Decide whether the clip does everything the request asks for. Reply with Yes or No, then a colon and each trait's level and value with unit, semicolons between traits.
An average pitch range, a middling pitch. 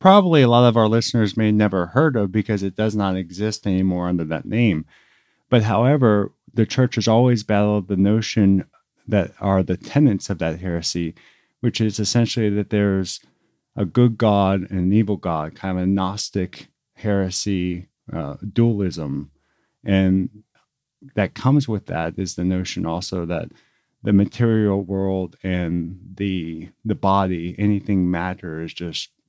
No: average, 3.0 semitones; low, 100 Hz